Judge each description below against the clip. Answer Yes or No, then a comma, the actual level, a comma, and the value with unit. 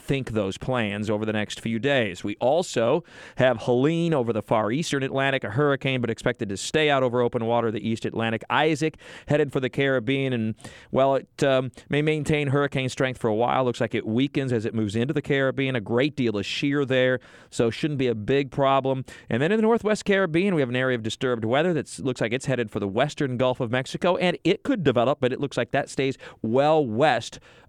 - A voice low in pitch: Yes, low, 130 Hz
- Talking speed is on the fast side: Yes, fast, 225 wpm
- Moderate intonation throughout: Yes, average, 3.4 semitones